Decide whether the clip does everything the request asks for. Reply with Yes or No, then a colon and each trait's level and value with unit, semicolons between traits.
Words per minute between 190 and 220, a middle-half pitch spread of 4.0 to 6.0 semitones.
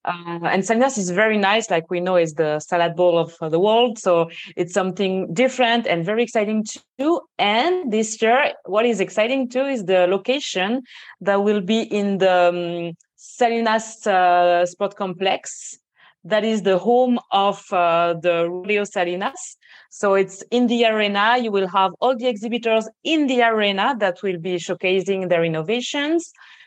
No: average, 165 wpm; average, 4.7 semitones